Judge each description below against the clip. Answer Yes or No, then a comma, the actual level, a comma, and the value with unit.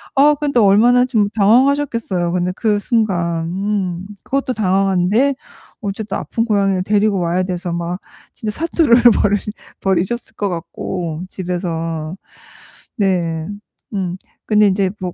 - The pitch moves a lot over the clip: No, average, 3.7 semitones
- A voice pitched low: No, high, 195 Hz